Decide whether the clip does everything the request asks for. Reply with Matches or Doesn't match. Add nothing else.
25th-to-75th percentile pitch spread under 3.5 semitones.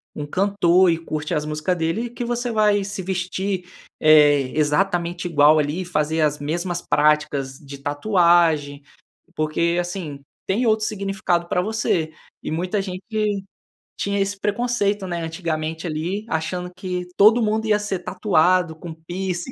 Doesn't match